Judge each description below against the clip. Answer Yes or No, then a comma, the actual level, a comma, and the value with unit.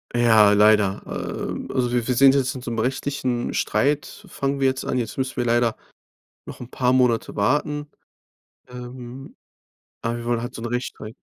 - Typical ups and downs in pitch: No, narrow, 2.1 semitones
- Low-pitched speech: Yes, low, 125 Hz